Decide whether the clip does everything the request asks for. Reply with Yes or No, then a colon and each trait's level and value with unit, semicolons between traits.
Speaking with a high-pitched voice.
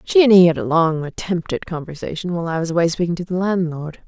No: medium, 170 Hz